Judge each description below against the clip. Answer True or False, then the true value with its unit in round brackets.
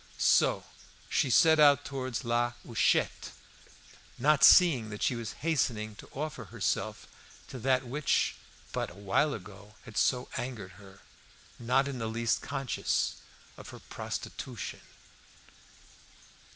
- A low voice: True (125 Hz)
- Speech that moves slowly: True (125 wpm)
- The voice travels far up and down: False (4.0 semitones)